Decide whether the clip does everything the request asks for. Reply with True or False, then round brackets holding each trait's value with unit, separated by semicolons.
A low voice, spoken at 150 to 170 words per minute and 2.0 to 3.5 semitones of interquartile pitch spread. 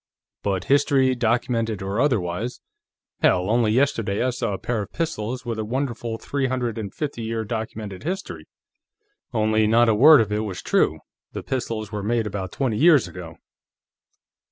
True (115 Hz; 165 wpm; 3.2 semitones)